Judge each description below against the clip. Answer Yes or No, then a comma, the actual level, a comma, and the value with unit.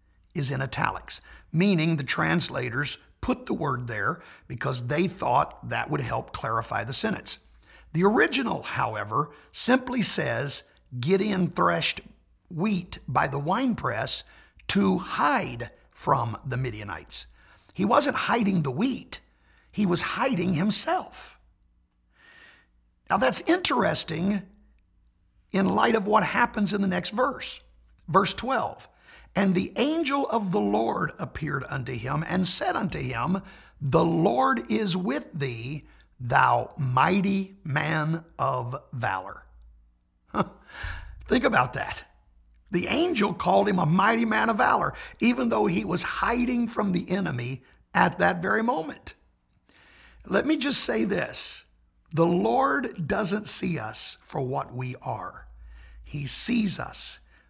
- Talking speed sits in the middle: No, slow, 125 wpm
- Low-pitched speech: No, medium, 170 Hz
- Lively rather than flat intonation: Yes, wide, 8.2 semitones